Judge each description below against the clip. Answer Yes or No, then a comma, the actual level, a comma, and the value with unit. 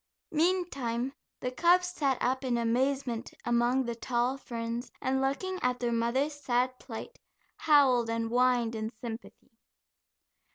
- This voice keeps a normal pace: No, slow, 130 wpm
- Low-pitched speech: No, very high, 250 Hz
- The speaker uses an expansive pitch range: No, narrow, 2.5 semitones